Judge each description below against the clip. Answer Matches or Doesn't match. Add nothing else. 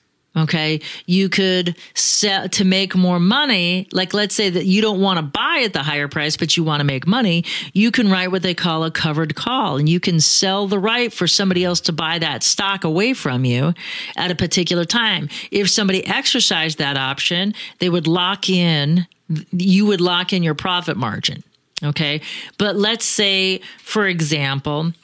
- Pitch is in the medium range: Matches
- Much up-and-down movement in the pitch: Doesn't match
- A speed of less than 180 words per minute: Doesn't match